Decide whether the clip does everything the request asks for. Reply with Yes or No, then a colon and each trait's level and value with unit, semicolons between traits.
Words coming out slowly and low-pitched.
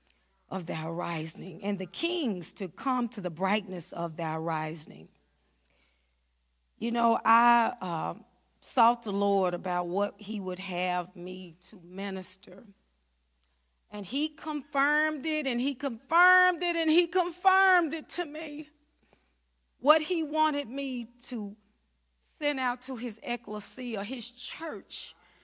No: slow, 130 wpm; high, 215 Hz